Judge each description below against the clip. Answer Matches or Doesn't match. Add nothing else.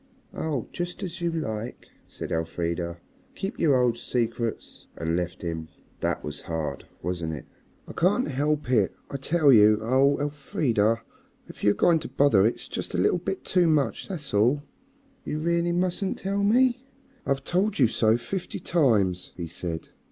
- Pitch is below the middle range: Matches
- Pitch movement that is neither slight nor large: Doesn't match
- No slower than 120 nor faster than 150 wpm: Doesn't match